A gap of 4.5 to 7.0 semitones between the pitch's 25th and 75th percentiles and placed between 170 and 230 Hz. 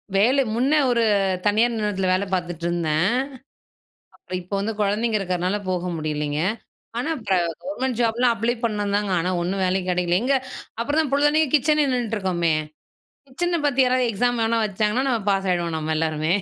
Yes: wide, 5.4 semitones; high, 210 Hz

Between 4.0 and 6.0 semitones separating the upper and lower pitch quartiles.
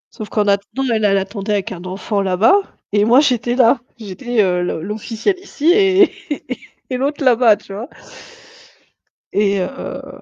Yes: average, 4.6 semitones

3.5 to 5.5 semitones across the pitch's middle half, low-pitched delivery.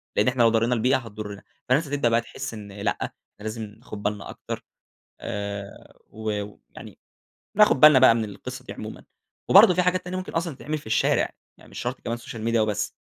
Yes: average, 4.3 semitones; low, 115 Hz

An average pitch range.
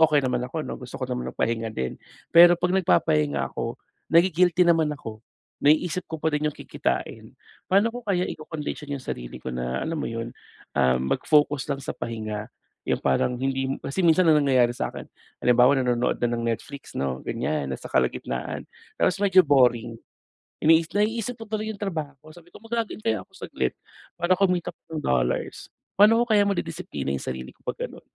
No: wide, 7.4 semitones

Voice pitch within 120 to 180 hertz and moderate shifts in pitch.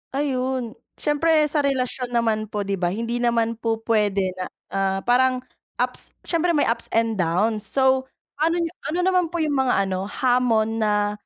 No: high, 235 Hz; average, 3.9 semitones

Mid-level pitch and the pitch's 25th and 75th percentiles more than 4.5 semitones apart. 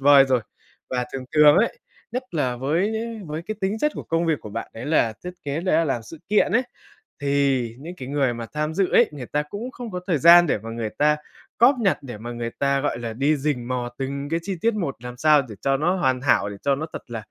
Yes: medium, 145 Hz; average, 5.1 semitones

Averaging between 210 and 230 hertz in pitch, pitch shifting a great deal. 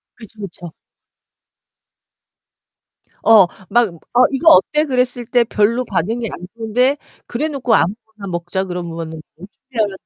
No: high, 225 Hz; average, 4.8 semitones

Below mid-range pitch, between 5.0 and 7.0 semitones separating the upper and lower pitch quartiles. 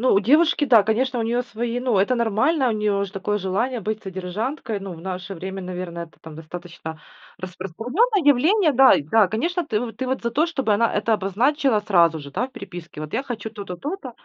No: high, 215 Hz; wide, 5.4 semitones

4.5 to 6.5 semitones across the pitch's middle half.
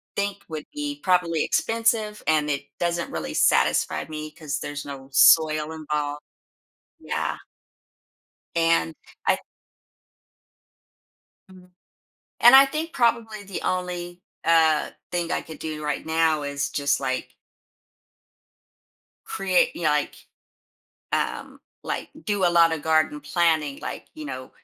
Yes: average, 4.8 semitones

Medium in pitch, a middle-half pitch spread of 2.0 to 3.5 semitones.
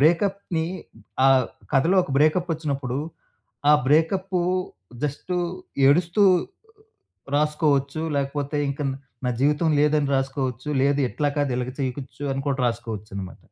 Yes: medium, 145 Hz; average, 3.2 semitones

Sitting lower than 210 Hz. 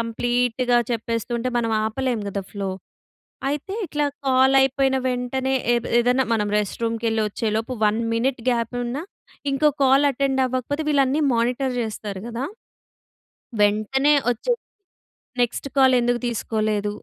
No: high, 245 Hz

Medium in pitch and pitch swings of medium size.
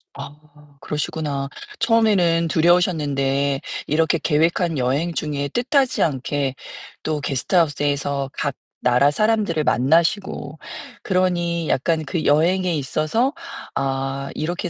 Yes: medium, 155 Hz; average, 3.6 semitones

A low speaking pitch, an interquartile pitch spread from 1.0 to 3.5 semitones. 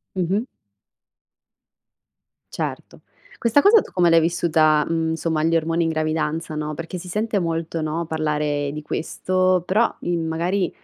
No: medium, 165 Hz; narrow, 2.5 semitones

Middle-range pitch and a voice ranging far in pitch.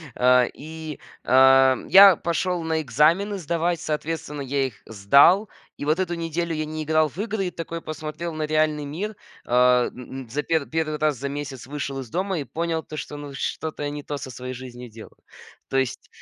No: medium, 150 Hz; average, 3.8 semitones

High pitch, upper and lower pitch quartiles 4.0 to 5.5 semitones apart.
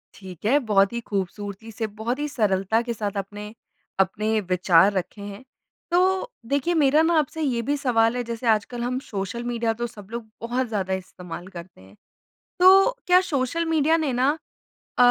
Yes: high, 225 Hz; average, 4.7 semitones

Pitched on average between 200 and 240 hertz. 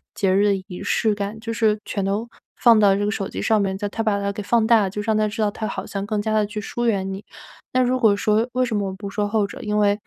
Yes: high, 210 Hz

